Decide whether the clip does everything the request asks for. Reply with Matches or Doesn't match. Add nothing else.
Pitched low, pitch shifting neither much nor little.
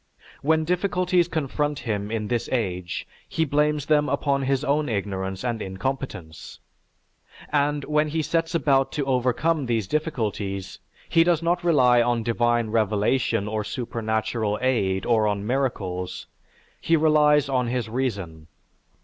Doesn't match